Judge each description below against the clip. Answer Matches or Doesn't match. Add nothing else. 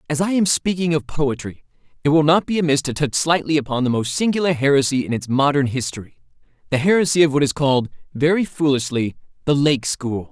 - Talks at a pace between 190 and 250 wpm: Matches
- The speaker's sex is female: Doesn't match